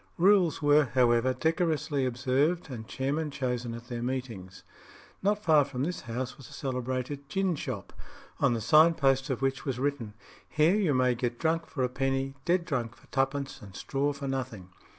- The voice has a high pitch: No, low, 135 Hz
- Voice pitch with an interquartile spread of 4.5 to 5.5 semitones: No, average, 3.5 semitones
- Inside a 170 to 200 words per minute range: Yes, average, 180 wpm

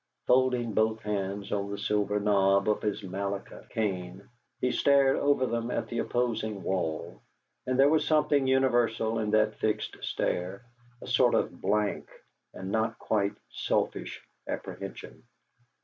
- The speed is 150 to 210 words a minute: No, average, 140 wpm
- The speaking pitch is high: No, low, 110 Hz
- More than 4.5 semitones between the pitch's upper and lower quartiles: No, average, 3.6 semitones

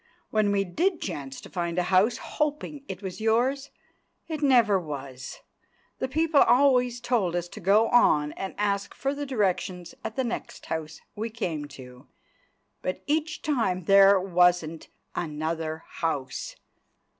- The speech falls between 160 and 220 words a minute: No, average, 145 wpm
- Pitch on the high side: Yes, high, 195 Hz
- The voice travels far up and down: Yes, wide, 6.9 semitones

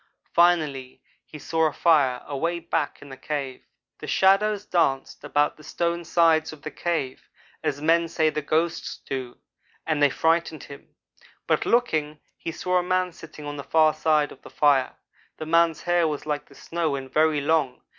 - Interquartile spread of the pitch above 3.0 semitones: No, narrow, 2.6 semitones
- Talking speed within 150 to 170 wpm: No, average, 180 wpm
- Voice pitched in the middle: Yes, medium, 155 Hz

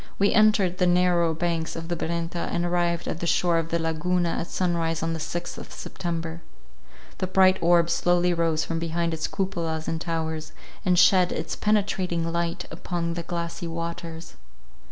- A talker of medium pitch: Yes, medium, 170 Hz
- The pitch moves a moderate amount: No, narrow, 1.2 semitones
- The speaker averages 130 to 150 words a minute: No, average, 175 wpm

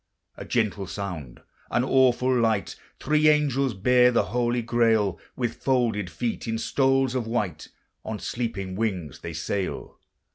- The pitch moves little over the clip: No, average, 4.1 semitones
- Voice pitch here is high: No, low, 115 Hz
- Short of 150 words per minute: Yes, average, 140 wpm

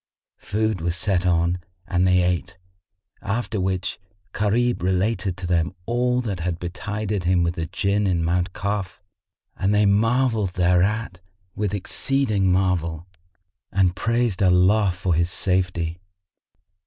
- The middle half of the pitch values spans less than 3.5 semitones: Yes, average, 2.9 semitones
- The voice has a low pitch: Yes, very low, 95 Hz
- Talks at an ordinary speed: No, slow, 130 wpm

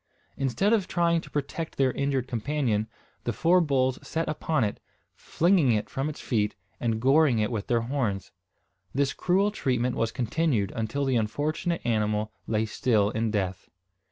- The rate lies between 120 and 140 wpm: No, average, 160 wpm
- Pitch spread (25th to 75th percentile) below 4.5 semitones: No, wide, 5.6 semitones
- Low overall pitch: Yes, low, 130 Hz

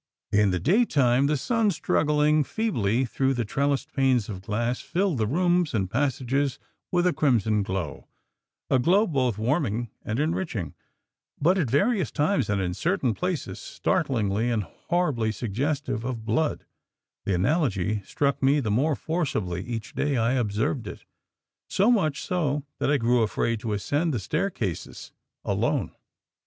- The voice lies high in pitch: No, low, 135 Hz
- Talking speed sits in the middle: Yes, average, 150 wpm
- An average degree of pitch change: No, wide, 6.1 semitones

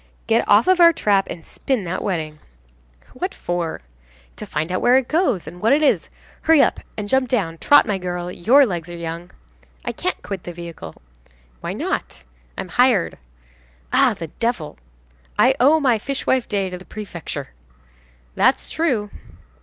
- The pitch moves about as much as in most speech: No, wide, 6.8 semitones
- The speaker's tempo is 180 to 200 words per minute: No, average, 170 wpm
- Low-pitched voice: No, high, 205 Hz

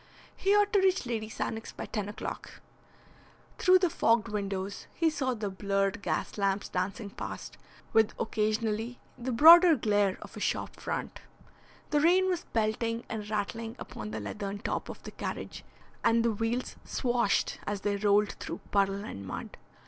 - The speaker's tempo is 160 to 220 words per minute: Yes, average, 165 wpm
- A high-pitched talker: Yes, high, 220 Hz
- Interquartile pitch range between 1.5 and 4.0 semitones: Yes, average, 3.4 semitones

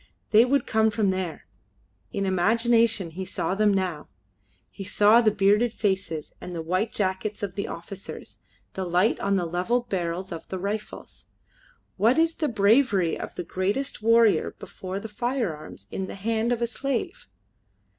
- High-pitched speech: Yes, high, 200 Hz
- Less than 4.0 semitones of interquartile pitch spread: Yes, average, 3.5 semitones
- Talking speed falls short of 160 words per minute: No, average, 165 wpm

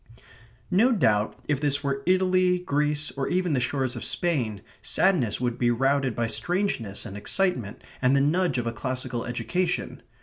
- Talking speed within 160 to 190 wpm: Yes, average, 165 wpm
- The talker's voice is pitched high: No, medium, 140 Hz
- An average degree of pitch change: No, wide, 6.8 semitones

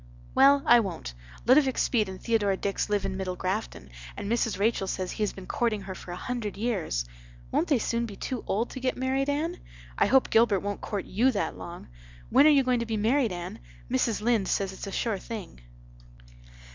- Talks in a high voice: Yes, high, 215 Hz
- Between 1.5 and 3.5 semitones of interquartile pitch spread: No, average, 4.2 semitones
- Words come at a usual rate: No, fast, 210 wpm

